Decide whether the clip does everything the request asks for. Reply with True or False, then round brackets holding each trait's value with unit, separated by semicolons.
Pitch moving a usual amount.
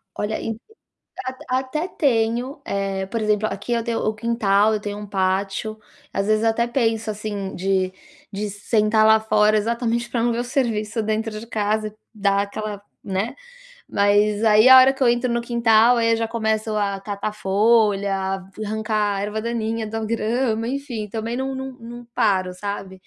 False (2.3 semitones)